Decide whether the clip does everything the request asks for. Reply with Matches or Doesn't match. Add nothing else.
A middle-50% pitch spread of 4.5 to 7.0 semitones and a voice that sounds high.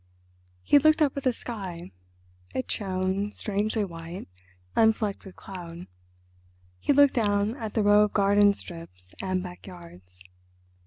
Doesn't match